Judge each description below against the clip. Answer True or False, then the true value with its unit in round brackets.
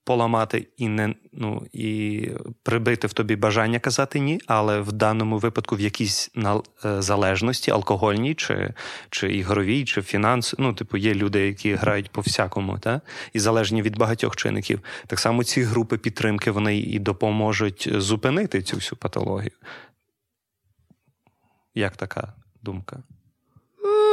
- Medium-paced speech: True (130 wpm)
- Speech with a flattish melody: True (2.0 semitones)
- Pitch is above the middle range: False (110 Hz)